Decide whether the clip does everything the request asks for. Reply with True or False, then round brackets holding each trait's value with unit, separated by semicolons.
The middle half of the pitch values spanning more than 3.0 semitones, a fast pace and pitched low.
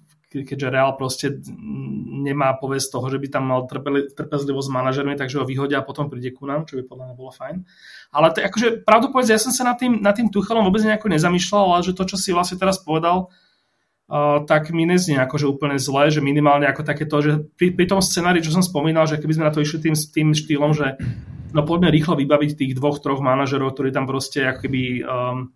False (4.4 semitones; 220 wpm; 150 Hz)